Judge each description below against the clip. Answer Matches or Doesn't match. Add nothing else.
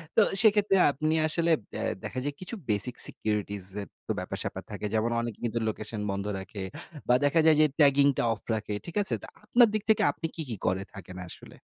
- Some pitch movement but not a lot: Doesn't match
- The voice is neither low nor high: Doesn't match